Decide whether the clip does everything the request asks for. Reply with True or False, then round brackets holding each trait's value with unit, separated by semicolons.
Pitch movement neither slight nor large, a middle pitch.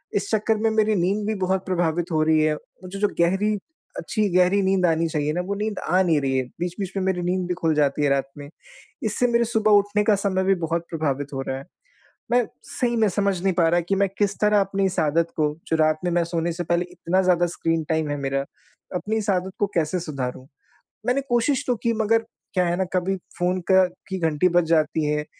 True (3.8 semitones; 180 Hz)